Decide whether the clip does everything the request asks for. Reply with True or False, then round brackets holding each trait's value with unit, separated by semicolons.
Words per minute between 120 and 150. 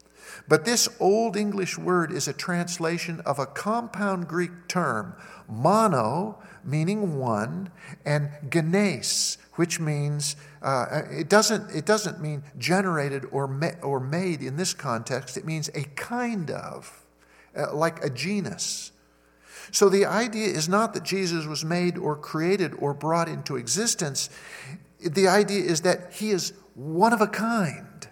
True (145 wpm)